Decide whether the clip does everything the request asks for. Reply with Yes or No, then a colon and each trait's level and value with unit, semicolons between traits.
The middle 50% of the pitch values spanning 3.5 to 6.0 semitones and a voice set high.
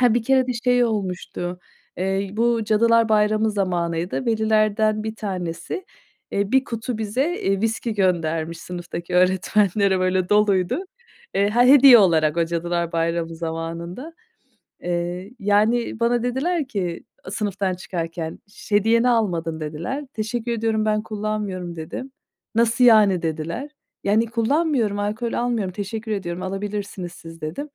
Yes: average, 4.6 semitones; high, 205 Hz